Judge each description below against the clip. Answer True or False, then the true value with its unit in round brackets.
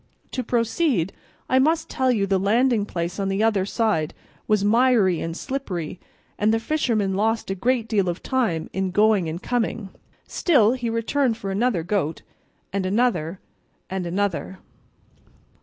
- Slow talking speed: False (155 wpm)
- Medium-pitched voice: False (210 Hz)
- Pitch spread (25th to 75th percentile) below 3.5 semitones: False (4.1 semitones)